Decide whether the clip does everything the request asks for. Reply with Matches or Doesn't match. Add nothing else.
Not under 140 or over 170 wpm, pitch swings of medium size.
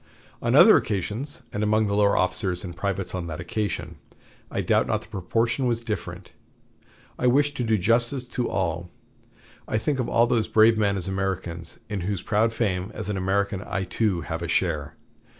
Doesn't match